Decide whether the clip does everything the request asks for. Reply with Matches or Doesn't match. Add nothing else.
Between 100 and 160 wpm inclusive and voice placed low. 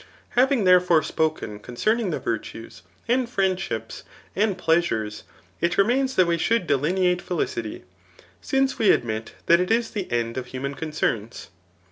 Doesn't match